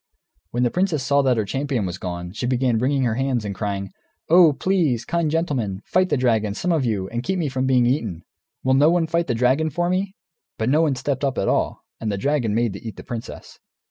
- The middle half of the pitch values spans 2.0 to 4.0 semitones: No, wide, 5.5 semitones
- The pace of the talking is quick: Yes, fast, 235 wpm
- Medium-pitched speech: No, low, 130 Hz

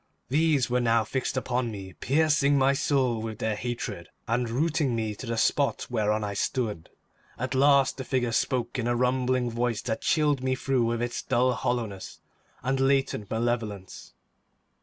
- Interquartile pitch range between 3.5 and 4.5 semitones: No, average, 2.8 semitones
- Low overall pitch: Yes, low, 125 Hz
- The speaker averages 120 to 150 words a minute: No, average, 165 wpm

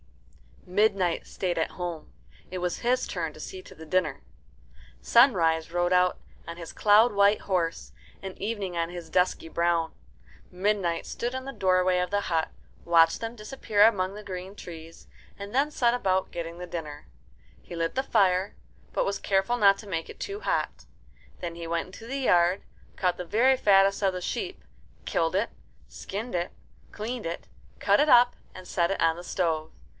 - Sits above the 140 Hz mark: Yes, medium, 185 Hz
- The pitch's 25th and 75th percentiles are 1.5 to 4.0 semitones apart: Yes, average, 3.6 semitones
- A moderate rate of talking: Yes, average, 180 wpm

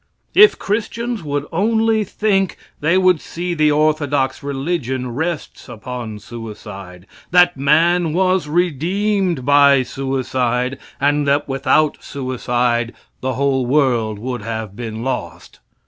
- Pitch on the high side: No, medium, 140 Hz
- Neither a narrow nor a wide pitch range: No, wide, 5.8 semitones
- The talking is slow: Yes, slow, 115 wpm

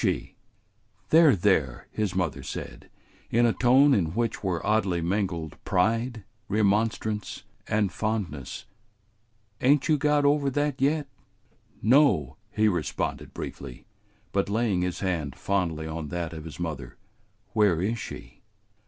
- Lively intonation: Yes, wide, 6.0 semitones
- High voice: No, low, 100 Hz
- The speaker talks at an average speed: No, slow, 125 wpm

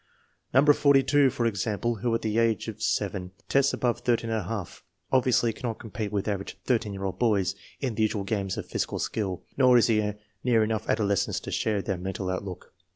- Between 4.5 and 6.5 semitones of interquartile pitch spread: No, average, 3.0 semitones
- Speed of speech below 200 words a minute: Yes, average, 190 wpm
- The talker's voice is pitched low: Yes, low, 110 Hz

